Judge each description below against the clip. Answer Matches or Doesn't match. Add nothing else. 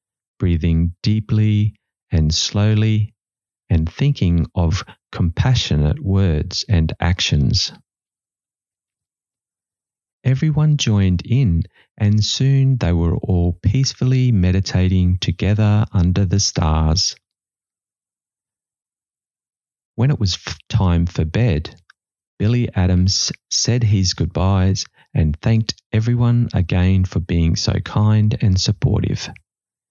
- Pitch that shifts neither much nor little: Matches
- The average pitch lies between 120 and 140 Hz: Doesn't match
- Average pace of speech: Doesn't match